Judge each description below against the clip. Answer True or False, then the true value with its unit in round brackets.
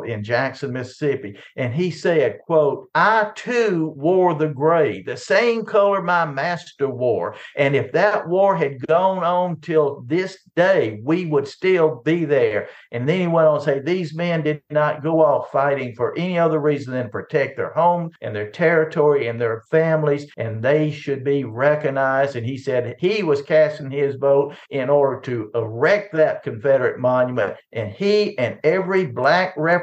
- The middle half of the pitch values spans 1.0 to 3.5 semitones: False (4.1 semitones)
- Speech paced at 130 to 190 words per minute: True (175 wpm)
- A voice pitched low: False (155 Hz)